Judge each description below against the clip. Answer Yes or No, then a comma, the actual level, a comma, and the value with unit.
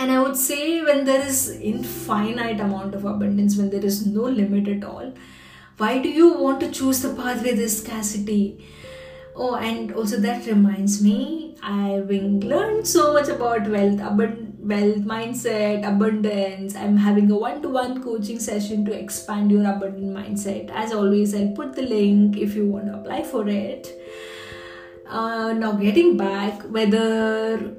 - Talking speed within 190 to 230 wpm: No, average, 160 wpm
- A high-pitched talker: Yes, high, 210 Hz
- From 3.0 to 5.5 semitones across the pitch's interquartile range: No, narrow, 2.5 semitones